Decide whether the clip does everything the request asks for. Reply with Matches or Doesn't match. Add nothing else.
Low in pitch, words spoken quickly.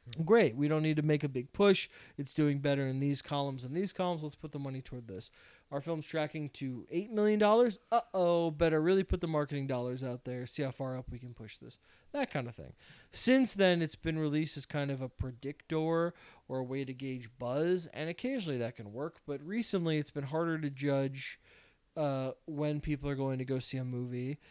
Doesn't match